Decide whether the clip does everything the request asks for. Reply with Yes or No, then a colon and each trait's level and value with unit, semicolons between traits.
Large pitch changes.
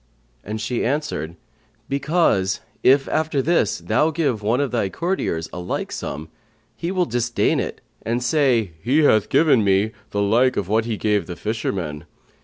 Yes: wide, 5.9 semitones